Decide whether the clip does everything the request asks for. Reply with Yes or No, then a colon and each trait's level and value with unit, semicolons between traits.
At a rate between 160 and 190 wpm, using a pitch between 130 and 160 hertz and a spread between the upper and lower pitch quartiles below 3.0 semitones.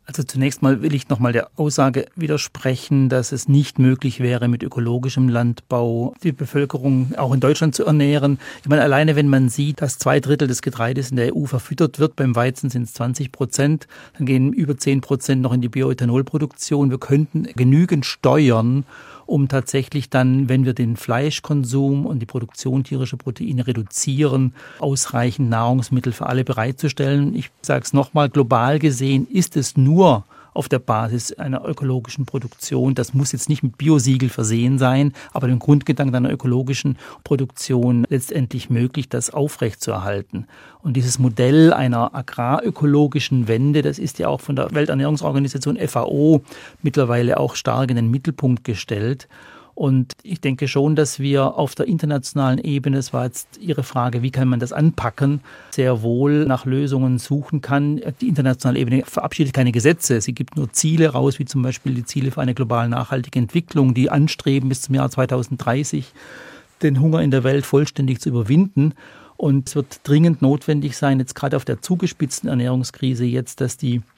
Yes: average, 165 wpm; low, 135 Hz; narrow, 2.4 semitones